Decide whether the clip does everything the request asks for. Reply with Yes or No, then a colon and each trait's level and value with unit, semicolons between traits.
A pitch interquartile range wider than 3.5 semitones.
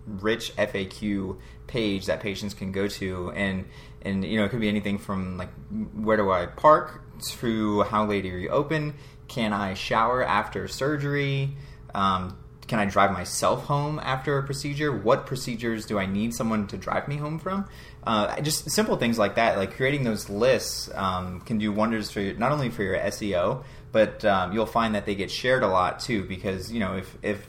Yes: average, 5.2 semitones